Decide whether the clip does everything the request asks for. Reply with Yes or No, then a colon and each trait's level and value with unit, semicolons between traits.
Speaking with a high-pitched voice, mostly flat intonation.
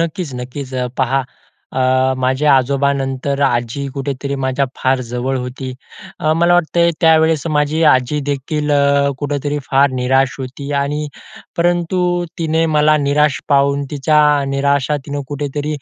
No: medium, 140 Hz; narrow, 2.2 semitones